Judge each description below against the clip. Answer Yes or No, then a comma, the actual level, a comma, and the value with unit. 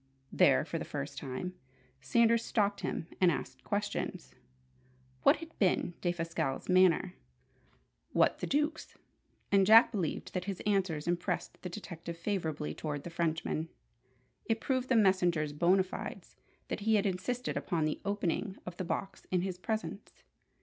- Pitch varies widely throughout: No, average, 3.6 semitones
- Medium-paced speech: Yes, average, 150 wpm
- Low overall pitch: No, medium, 185 Hz